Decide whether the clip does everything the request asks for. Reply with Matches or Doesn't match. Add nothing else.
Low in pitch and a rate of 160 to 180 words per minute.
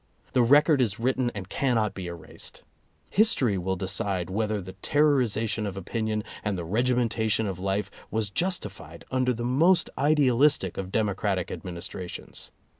Doesn't match